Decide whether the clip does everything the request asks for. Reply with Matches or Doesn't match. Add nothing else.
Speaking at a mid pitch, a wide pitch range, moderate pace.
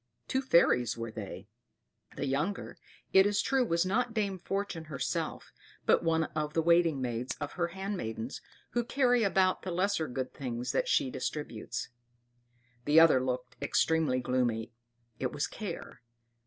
Matches